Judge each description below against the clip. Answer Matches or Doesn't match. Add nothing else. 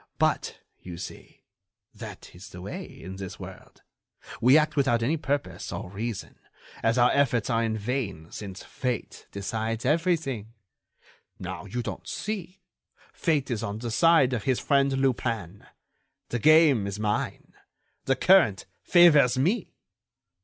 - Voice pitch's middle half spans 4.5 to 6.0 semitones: Matches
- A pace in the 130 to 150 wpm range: Matches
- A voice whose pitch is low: Matches